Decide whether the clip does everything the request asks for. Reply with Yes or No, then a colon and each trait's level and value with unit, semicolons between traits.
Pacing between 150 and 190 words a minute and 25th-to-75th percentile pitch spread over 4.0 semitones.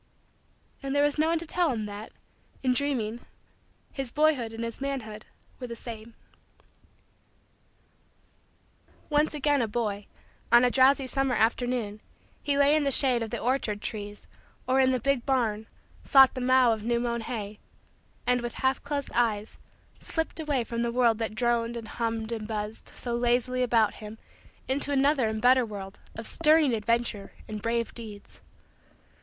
No: average, 165 wpm; average, 3.4 semitones